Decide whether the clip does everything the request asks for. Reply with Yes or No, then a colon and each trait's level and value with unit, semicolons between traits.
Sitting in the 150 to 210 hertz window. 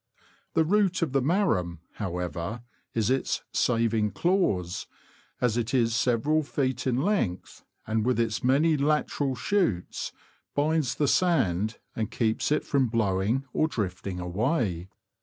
No: low, 120 Hz